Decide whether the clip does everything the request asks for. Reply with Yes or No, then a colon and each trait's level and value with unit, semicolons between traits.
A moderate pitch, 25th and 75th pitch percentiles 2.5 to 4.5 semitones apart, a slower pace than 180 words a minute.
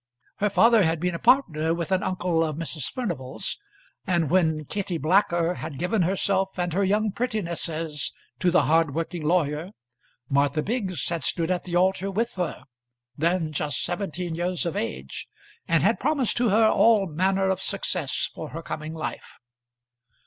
Yes: medium, 175 Hz; average, 3.4 semitones; average, 165 wpm